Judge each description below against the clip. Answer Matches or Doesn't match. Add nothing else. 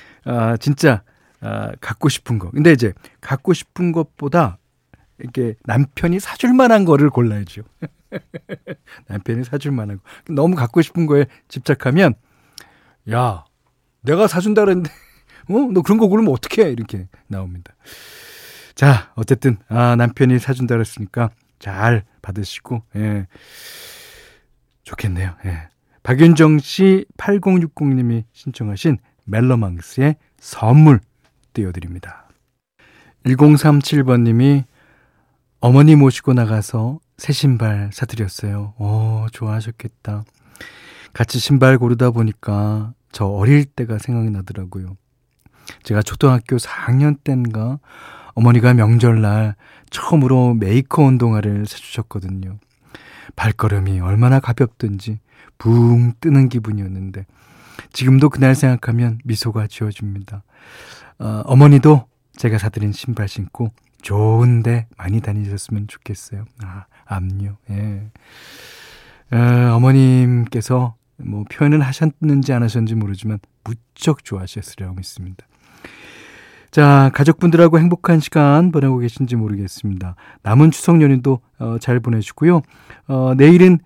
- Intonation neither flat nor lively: Matches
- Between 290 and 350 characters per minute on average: Doesn't match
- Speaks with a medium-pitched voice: Doesn't match